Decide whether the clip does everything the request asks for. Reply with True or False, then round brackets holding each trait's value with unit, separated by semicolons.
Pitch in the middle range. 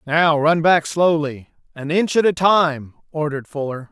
True (155 Hz)